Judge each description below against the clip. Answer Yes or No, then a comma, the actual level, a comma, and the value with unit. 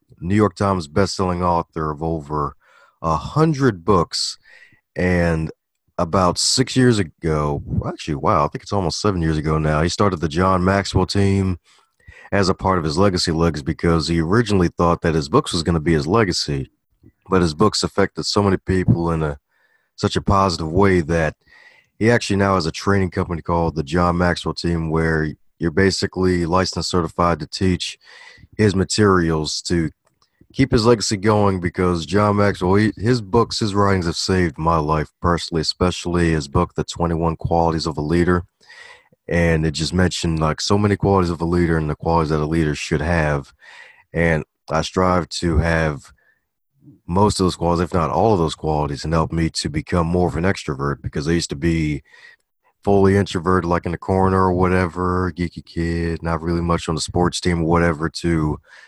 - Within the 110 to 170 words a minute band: No, average, 185 wpm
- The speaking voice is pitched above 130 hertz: No, very low, 85 Hz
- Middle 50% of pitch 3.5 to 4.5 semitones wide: No, average, 2.8 semitones